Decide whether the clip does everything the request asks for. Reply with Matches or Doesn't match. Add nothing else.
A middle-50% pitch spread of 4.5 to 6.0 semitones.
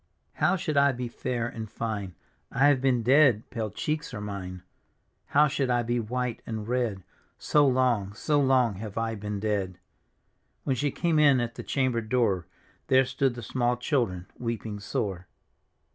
Doesn't match